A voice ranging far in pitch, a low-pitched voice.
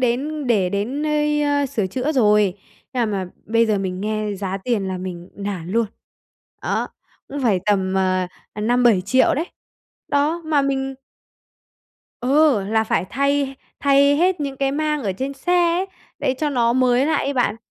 No: wide, 5.9 semitones; very high, 250 Hz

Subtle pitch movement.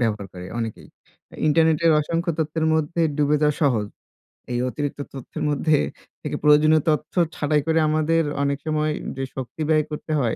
Yes: narrow, 2.1 semitones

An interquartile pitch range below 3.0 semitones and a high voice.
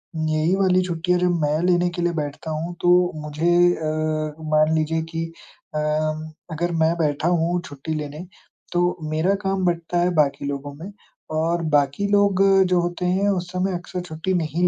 No: narrow, 2.5 semitones; medium, 165 Hz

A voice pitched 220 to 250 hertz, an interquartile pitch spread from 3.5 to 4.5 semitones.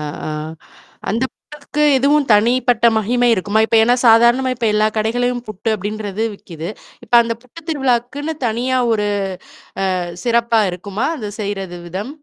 No: high, 230 Hz; average, 3.1 semitones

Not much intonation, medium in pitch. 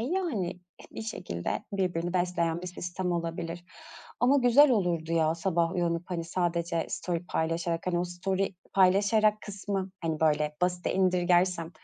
Yes: narrow, 2.3 semitones; medium, 175 Hz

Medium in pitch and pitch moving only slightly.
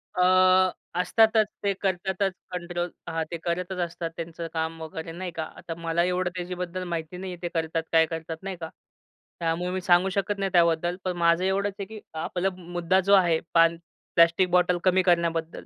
Yes: medium, 175 Hz; narrow, 1.9 semitones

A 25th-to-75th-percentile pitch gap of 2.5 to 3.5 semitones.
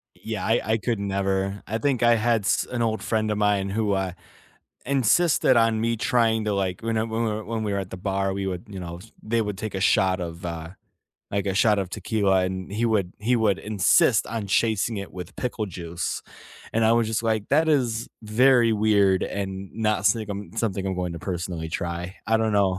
Yes: average, 2.8 semitones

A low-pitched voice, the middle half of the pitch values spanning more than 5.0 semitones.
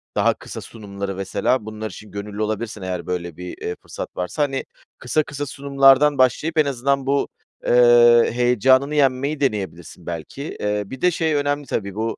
Yes: low, 120 Hz; wide, 5.5 semitones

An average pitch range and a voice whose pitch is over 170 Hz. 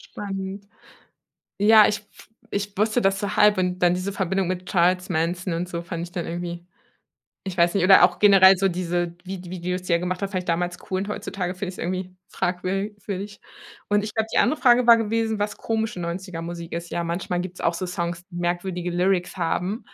No: narrow, 2.3 semitones; medium, 185 Hz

